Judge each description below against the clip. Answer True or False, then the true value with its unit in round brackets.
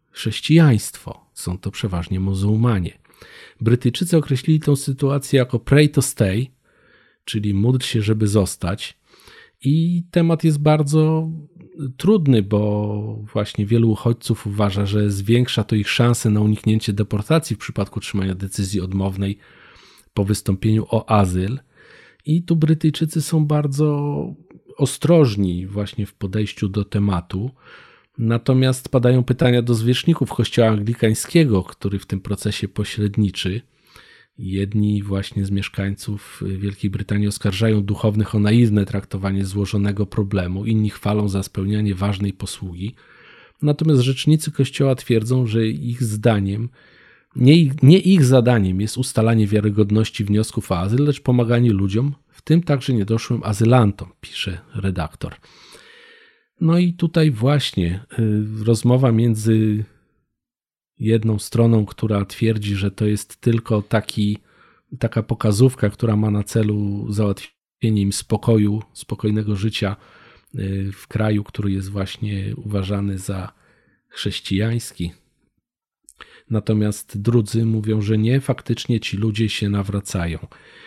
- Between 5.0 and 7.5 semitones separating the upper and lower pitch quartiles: False (3.8 semitones)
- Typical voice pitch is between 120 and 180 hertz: False (110 Hz)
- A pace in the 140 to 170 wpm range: False (115 wpm)